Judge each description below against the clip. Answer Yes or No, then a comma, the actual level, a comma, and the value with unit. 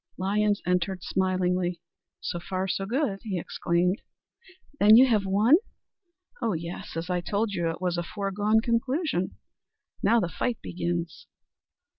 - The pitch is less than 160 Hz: No, high, 190 Hz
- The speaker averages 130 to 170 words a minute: Yes, average, 140 wpm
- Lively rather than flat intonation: No, average, 3.4 semitones